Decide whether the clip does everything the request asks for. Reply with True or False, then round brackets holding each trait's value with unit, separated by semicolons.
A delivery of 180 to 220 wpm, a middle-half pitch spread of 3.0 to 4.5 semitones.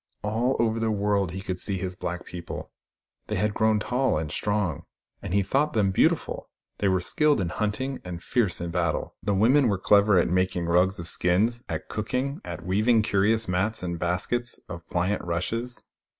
True (185 wpm; 4.1 semitones)